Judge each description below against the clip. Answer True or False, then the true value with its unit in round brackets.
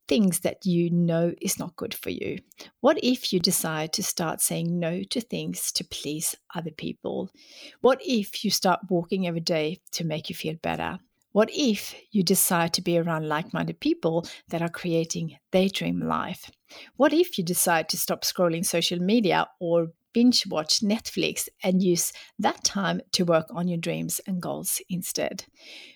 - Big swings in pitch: False (3.8 semitones)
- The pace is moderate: True (175 wpm)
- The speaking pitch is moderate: True (180 Hz)